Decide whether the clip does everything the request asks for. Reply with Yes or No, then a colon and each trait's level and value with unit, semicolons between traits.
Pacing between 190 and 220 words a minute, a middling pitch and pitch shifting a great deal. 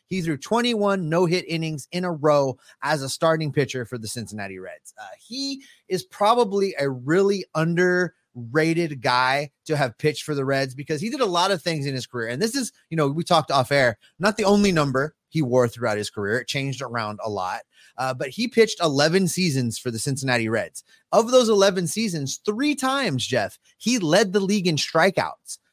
Yes: fast, 205 wpm; medium, 160 Hz; wide, 6.8 semitones